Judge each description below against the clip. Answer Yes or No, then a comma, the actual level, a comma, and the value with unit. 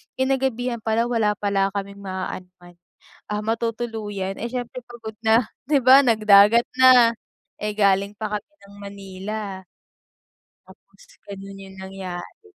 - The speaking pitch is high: Yes, high, 210 Hz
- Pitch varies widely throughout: No, average, 3.0 semitones